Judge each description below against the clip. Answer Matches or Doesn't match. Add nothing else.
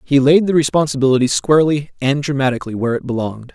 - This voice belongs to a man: Matches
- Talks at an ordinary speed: Matches